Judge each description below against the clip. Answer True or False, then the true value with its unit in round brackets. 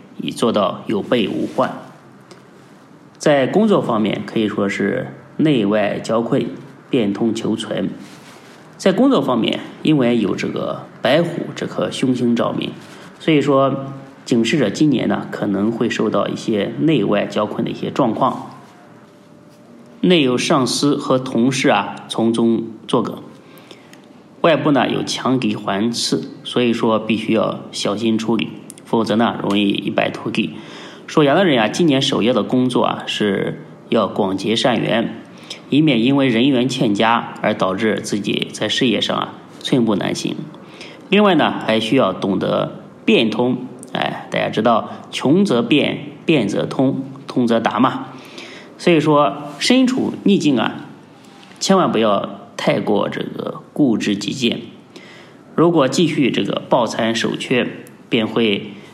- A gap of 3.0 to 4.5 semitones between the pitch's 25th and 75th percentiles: True (3.7 semitones)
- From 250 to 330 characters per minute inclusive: False (210 characters per minute)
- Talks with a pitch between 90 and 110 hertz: False (120 Hz)